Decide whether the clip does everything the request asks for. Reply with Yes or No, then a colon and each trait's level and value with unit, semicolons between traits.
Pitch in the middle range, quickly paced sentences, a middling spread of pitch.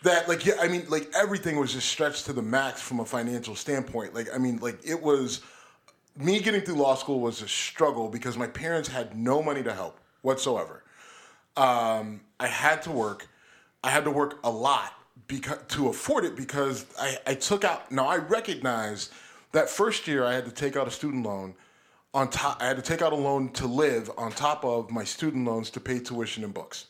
No: low, 130 Hz; fast, 215 wpm; average, 3.9 semitones